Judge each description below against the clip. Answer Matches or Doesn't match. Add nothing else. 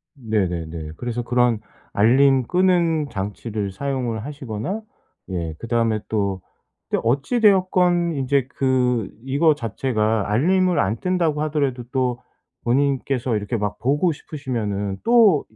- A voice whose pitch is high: Doesn't match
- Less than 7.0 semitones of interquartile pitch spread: Matches